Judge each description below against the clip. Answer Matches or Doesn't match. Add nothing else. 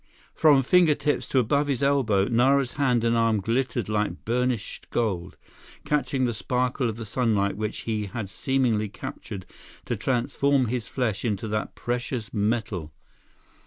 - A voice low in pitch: Matches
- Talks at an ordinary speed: Matches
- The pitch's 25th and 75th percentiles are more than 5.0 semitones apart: Doesn't match